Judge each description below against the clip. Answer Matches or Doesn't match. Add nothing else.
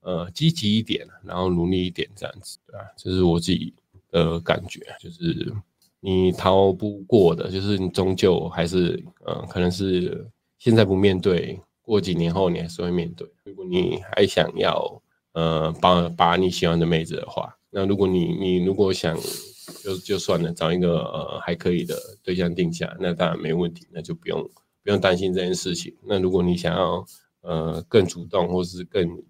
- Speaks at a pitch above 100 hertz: Doesn't match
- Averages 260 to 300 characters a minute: Matches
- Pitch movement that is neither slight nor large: Doesn't match